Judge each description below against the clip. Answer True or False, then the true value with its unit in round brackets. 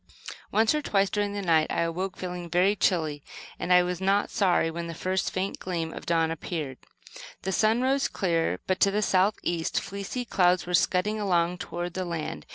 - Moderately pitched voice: True (180 Hz)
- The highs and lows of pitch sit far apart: False (2.8 semitones)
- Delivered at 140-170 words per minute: False (195 wpm)